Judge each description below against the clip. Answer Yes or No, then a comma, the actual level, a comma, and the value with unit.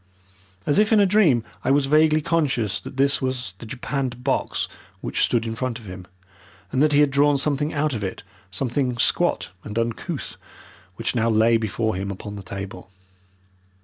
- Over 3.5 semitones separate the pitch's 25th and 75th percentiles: Yes, average, 4.7 semitones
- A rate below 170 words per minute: No, average, 180 wpm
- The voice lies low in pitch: Yes, low, 125 Hz